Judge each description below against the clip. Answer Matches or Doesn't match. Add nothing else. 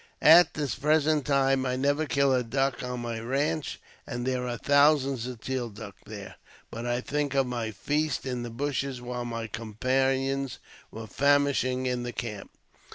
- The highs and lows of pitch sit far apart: Doesn't match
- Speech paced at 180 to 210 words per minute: Doesn't match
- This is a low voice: Matches